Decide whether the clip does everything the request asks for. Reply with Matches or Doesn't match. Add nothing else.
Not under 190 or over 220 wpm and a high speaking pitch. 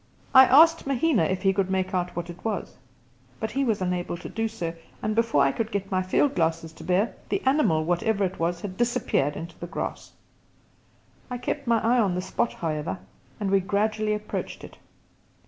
Matches